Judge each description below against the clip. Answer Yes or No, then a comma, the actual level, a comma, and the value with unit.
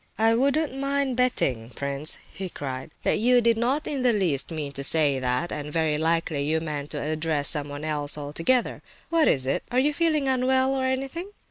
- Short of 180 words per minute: No, average, 195 wpm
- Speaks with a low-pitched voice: No, medium, 165 Hz